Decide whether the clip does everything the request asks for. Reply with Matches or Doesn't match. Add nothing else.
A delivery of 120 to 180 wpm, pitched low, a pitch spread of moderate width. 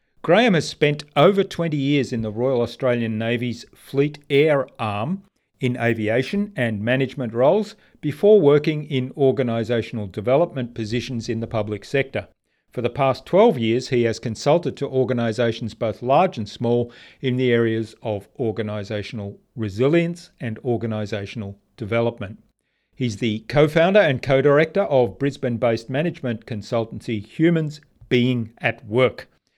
Matches